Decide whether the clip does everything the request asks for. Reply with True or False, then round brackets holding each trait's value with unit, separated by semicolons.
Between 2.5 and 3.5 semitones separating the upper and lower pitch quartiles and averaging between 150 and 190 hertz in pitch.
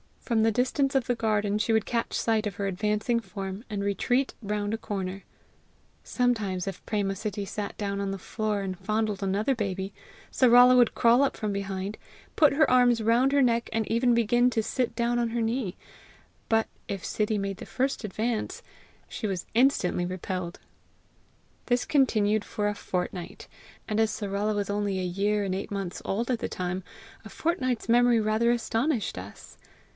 False (3.2 semitones; 215 Hz)